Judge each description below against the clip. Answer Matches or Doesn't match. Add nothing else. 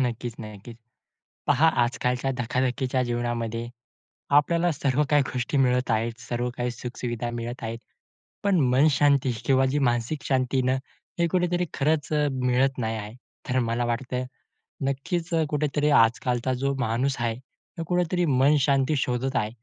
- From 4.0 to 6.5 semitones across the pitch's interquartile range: Doesn't match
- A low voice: Matches